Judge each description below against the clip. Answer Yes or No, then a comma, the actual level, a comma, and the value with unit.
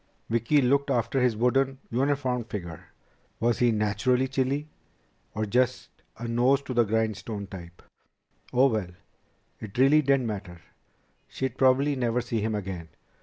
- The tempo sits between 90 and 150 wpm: Yes, average, 140 wpm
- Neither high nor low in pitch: No, low, 120 Hz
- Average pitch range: Yes, average, 3.6 semitones